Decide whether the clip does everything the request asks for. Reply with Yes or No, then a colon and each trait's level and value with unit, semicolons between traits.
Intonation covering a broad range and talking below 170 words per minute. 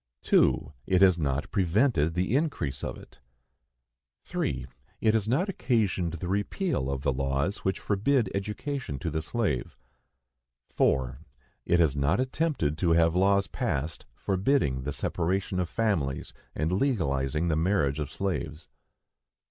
Yes: wide, 6.4 semitones; average, 140 wpm